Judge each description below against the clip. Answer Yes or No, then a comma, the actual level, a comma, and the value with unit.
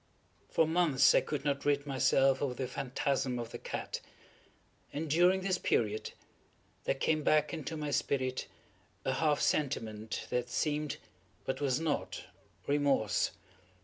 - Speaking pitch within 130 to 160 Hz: Yes, medium, 140 Hz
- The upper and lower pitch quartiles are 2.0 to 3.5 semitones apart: Yes, average, 2.8 semitones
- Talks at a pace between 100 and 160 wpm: Yes, average, 140 wpm